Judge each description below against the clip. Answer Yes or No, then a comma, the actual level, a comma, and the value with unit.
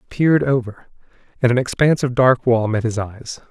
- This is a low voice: Yes, low, 125 Hz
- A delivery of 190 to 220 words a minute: Yes, fast, 205 wpm